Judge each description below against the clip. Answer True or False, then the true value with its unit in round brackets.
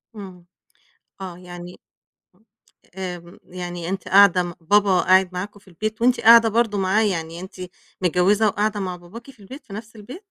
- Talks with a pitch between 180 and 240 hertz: True (190 Hz)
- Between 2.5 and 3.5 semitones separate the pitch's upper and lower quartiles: True (3.0 semitones)